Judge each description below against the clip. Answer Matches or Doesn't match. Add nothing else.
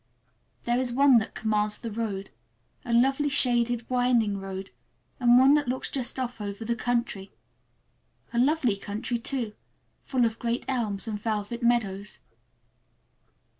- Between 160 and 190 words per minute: Doesn't match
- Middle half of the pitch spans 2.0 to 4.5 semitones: Matches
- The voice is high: Matches